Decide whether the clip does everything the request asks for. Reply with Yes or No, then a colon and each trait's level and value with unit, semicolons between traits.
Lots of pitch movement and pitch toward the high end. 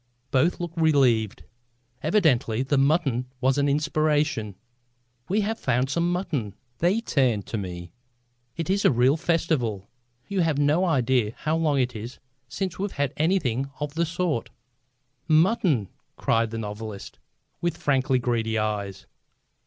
No: wide, 6.1 semitones; medium, 140 Hz